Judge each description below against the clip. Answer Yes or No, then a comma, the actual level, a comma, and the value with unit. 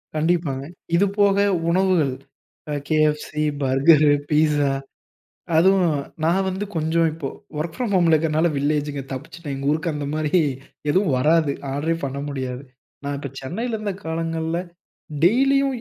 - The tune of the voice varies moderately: Yes, average, 3.4 semitones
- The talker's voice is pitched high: No, medium, 160 Hz